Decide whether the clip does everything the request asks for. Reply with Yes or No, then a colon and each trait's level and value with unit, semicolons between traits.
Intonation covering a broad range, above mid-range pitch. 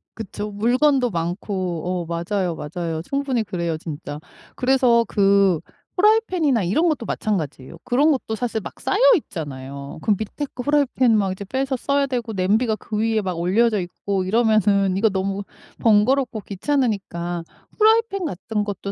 Yes: wide, 5.9 semitones; high, 210 Hz